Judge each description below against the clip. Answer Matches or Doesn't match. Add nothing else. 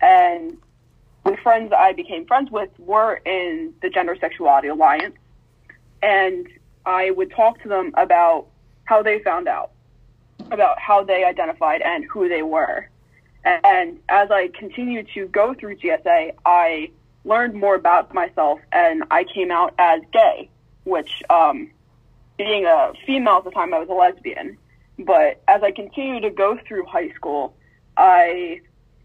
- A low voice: Doesn't match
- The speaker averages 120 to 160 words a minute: Matches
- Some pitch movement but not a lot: Doesn't match